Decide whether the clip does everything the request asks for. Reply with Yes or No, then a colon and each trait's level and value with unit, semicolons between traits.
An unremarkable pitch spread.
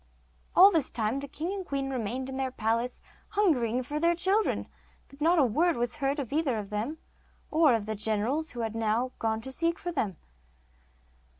No: wide, 5.8 semitones